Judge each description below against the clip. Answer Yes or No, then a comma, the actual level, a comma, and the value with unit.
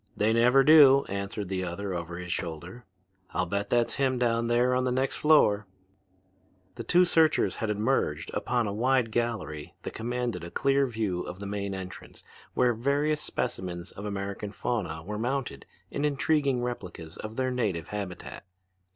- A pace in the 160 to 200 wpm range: Yes, average, 165 wpm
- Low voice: Yes, low, 110 Hz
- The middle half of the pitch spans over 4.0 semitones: Yes, average, 5.1 semitones